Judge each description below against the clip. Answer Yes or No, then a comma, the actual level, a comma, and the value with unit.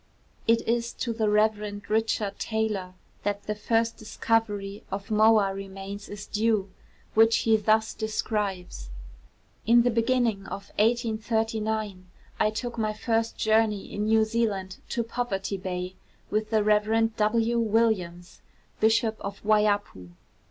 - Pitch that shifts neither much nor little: No, narrow, 1.9 semitones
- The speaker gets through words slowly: Yes, slow, 130 wpm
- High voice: Yes, high, 215 Hz